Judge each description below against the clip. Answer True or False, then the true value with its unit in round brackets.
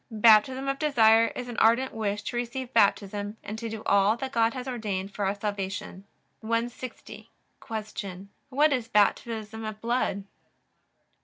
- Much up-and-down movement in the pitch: False (2.9 semitones)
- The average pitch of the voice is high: True (225 Hz)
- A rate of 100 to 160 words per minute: True (150 wpm)